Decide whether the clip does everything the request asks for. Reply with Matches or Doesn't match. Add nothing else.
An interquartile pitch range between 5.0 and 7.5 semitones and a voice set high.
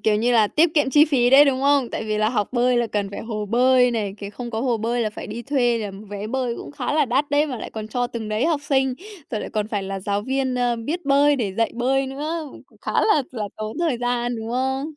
Doesn't match